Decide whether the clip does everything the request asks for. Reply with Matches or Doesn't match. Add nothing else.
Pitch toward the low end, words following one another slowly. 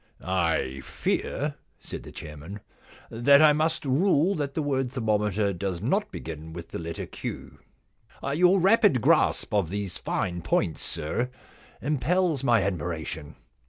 Doesn't match